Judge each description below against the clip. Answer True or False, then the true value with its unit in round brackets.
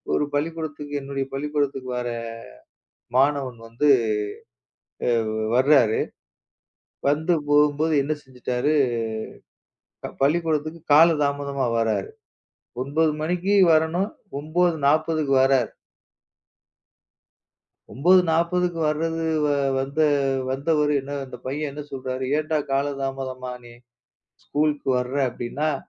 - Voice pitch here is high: False (145 Hz)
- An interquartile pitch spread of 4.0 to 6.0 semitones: False (2.8 semitones)